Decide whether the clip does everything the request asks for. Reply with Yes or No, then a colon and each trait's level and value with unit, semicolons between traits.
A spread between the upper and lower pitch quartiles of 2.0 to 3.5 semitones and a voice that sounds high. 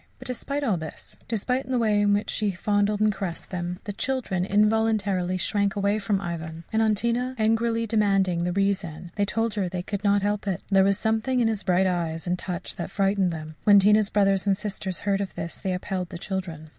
Yes: average, 2.8 semitones; high, 200 Hz